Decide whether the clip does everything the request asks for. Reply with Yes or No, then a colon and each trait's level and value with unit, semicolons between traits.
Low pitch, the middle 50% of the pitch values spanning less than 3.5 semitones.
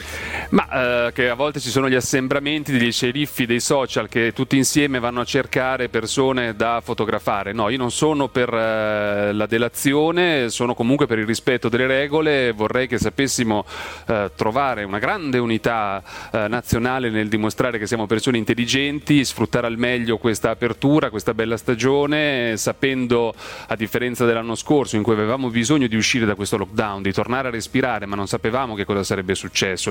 Yes: low, 120 Hz; average, 3.1 semitones